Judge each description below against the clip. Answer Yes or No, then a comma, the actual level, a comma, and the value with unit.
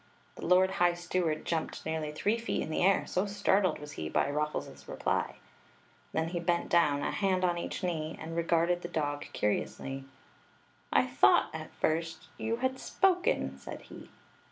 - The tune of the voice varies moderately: Yes, average, 3.2 semitones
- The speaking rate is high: No, average, 170 wpm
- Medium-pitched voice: Yes, medium, 170 Hz